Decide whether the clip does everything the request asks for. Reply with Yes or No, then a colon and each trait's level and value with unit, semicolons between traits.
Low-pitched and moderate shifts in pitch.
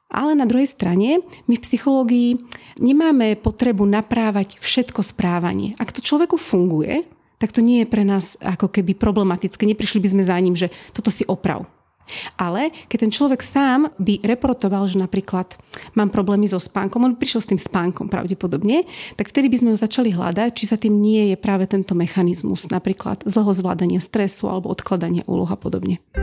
No: high, 210 Hz; average, 4.2 semitones